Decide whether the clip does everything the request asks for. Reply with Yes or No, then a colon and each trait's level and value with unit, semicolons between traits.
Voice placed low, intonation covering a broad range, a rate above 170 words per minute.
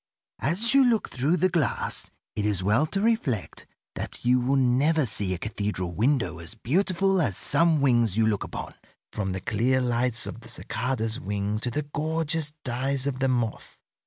Yes: low, 125 Hz; wide, 6.1 semitones; average, 180 wpm